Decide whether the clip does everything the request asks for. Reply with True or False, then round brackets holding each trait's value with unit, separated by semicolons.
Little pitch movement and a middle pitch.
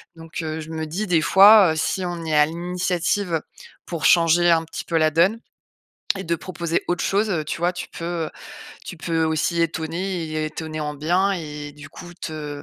True (2.0 semitones; 165 Hz)